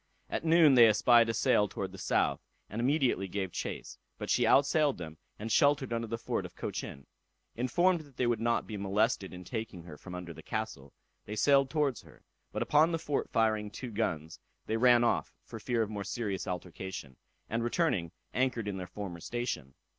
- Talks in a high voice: No, low, 115 Hz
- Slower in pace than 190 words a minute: No, average, 195 wpm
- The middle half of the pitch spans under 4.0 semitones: No, average, 5.0 semitones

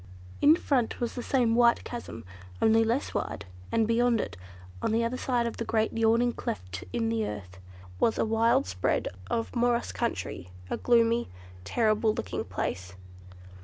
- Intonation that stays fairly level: Yes, narrow, 1.9 semitones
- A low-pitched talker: No, high, 230 Hz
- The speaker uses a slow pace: No, average, 160 wpm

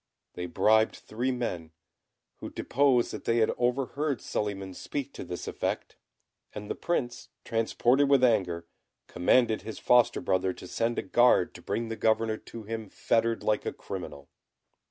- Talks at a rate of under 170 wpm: Yes, average, 155 wpm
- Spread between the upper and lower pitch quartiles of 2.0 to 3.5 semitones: No, average, 3.9 semitones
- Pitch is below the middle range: Yes, low, 115 Hz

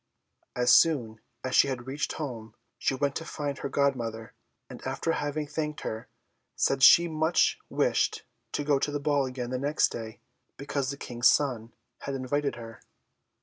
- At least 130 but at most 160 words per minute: No, average, 170 wpm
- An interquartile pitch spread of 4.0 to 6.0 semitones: No, average, 3.0 semitones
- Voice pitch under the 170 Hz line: Yes, medium, 140 Hz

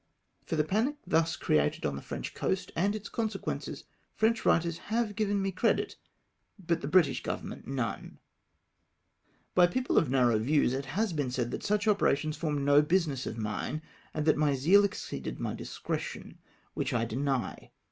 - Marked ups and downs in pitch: Yes, wide, 6.5 semitones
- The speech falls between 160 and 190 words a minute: Yes, average, 170 wpm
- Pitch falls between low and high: Yes, medium, 160 Hz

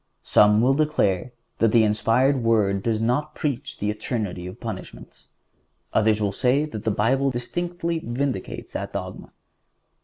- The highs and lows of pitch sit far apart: No, average, 4.6 semitones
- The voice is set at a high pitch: No, low, 115 Hz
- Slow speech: No, average, 145 wpm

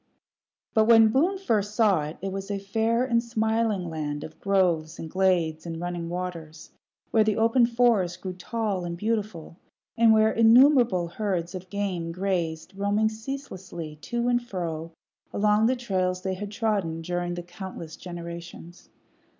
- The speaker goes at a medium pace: Yes, average, 150 wpm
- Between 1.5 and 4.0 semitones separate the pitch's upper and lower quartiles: No, average, 4.4 semitones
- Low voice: No, high, 190 Hz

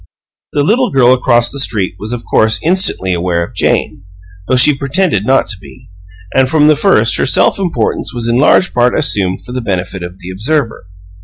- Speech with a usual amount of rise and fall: No, wide, 7.0 semitones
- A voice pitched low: Yes, low, 120 Hz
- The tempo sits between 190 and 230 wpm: Yes, average, 200 wpm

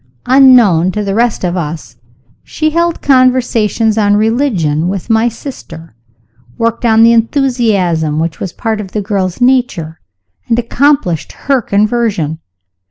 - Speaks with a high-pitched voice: Yes, high, 220 Hz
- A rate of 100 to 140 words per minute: Yes, slow, 135 wpm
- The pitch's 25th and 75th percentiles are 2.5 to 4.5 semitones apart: No, wide, 5.4 semitones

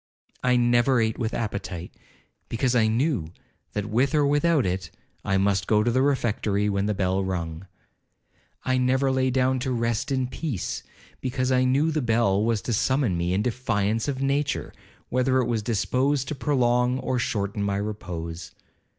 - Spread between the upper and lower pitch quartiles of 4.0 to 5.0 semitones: Yes, average, 4.3 semitones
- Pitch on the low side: Yes, low, 120 Hz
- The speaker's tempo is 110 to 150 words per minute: No, average, 170 wpm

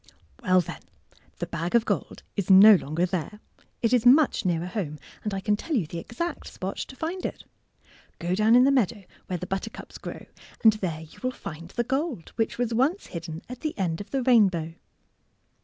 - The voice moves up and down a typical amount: No, wide, 5.9 semitones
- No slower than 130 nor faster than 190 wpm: No, average, 200 wpm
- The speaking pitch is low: No, high, 205 Hz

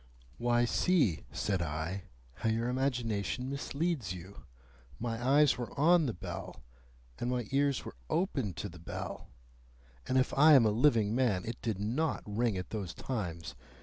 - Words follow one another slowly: No, average, 160 wpm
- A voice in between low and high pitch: No, low, 115 Hz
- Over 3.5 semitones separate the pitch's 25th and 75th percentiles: Yes, average, 5.1 semitones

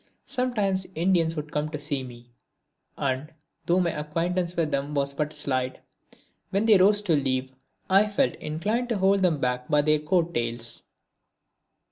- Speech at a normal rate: Yes, average, 160 wpm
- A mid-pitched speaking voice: Yes, medium, 155 Hz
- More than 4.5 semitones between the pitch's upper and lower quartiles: Yes, average, 5.2 semitones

